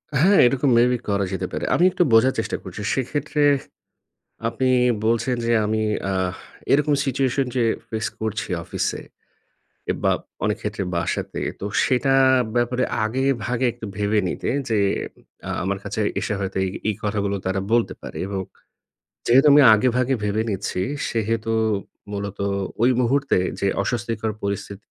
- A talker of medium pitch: No, low, 115 Hz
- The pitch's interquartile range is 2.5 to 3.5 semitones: No, average, 4.2 semitones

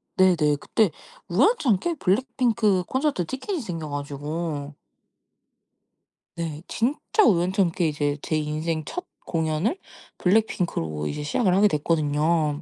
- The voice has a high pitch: No, medium, 170 Hz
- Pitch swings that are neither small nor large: No, wide, 6.3 semitones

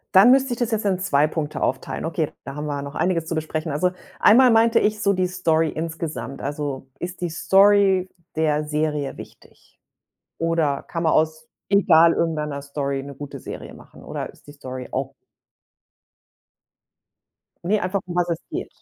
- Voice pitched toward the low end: No, medium, 160 Hz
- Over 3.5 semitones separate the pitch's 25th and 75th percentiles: Yes, average, 4.1 semitones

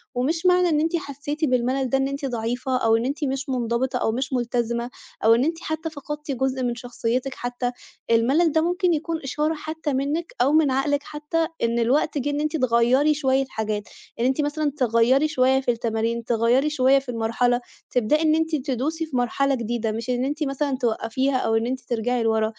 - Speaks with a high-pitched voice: Yes, very high, 265 Hz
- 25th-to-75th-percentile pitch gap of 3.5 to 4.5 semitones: Yes, average, 3.8 semitones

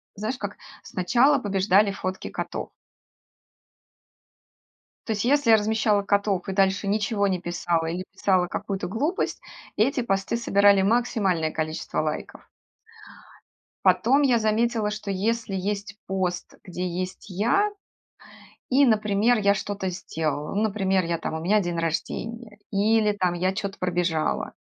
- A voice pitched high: Yes, high, 200 Hz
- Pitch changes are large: No, average, 3.1 semitones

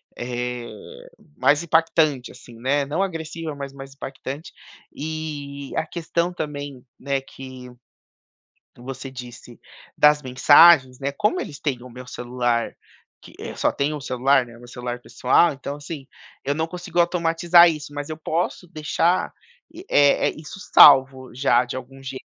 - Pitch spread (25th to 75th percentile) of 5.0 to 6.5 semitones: No, average, 3.7 semitones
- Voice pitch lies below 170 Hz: Yes, medium, 140 Hz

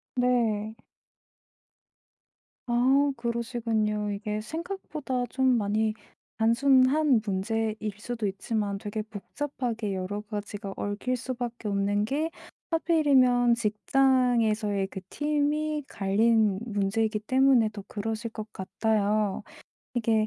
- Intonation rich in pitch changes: No, average, 3.5 semitones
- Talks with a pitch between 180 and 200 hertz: No, high, 225 Hz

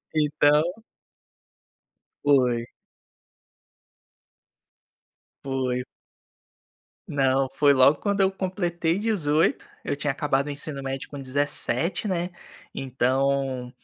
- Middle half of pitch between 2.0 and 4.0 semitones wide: Yes, average, 3.3 semitones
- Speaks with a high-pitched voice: No, medium, 145 Hz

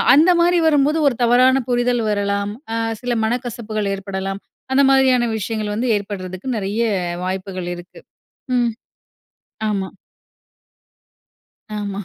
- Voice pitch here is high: Yes, high, 215 Hz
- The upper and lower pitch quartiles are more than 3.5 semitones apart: Yes, average, 4.0 semitones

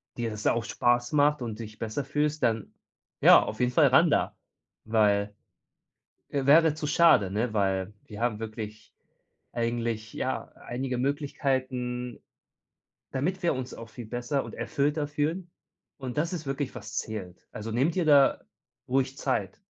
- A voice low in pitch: Yes, low, 125 Hz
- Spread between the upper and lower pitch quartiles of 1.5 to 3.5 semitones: No, average, 4.5 semitones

